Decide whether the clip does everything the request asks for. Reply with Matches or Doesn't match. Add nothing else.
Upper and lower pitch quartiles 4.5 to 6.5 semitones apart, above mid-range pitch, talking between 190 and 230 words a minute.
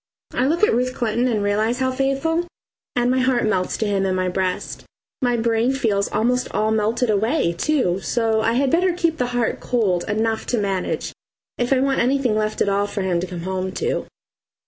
Doesn't match